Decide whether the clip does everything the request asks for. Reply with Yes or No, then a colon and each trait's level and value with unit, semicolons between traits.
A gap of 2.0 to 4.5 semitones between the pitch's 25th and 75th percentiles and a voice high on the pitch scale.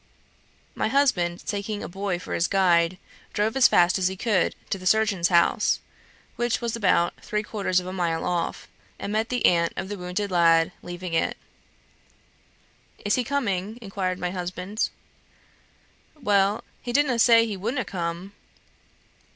Yes: average, 3.6 semitones; high, 195 Hz